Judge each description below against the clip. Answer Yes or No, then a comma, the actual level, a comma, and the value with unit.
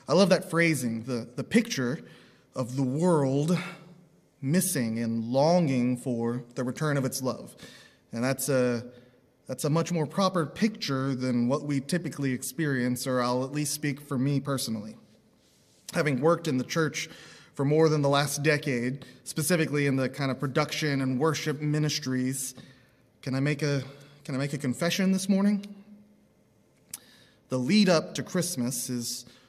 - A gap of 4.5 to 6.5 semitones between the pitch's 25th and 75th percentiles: No, average, 4.0 semitones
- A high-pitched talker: No, medium, 140 Hz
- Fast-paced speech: No, average, 160 wpm